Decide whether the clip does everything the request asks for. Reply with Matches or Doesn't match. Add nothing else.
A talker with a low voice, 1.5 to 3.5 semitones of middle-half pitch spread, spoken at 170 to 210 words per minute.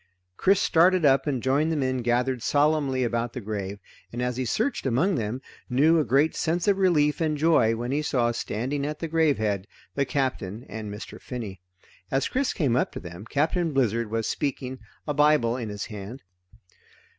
Doesn't match